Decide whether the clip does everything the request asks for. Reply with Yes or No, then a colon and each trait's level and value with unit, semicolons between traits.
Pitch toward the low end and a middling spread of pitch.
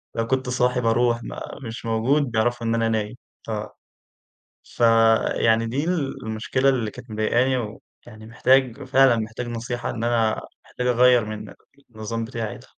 No: low, 115 Hz; narrow, 1.9 semitones